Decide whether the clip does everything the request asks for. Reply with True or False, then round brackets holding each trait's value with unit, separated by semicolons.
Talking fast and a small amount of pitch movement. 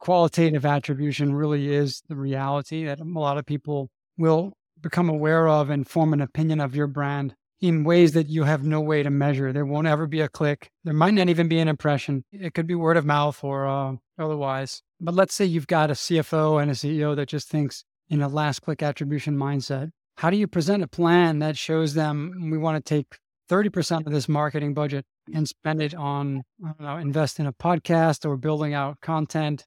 True (210 wpm; 2.2 semitones)